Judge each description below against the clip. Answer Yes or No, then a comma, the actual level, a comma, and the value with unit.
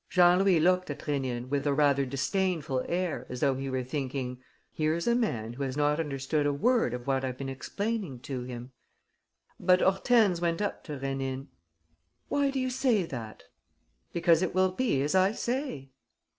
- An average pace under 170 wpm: No, average, 180 wpm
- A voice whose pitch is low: No, medium, 150 Hz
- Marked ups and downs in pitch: Yes, wide, 5.8 semitones